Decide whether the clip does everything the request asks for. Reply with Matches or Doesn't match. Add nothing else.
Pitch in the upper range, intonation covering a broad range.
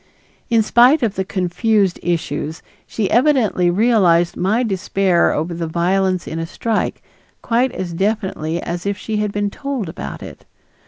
Doesn't match